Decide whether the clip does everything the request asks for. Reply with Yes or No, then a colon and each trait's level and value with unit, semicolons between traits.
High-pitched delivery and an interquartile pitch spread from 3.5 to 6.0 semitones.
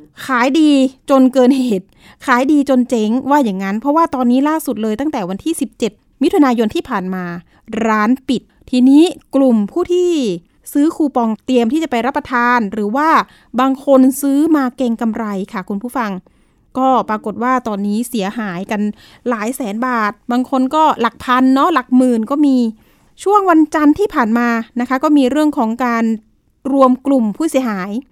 Yes: very high, 255 Hz; average, 3.8 semitones